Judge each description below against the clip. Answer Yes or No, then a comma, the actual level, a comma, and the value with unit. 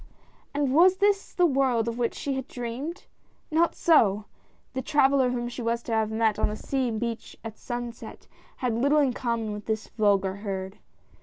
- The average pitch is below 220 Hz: No, high, 240 Hz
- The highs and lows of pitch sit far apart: No, average, 3.8 semitones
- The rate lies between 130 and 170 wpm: No, average, 180 wpm